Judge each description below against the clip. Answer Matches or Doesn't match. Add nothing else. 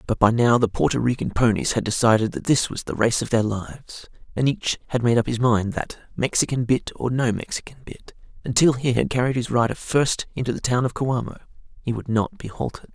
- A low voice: Matches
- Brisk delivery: Matches